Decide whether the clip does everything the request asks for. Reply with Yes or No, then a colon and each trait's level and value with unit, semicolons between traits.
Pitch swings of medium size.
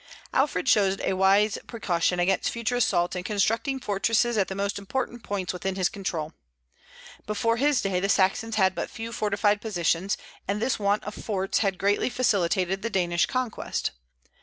Yes: average, 3.2 semitones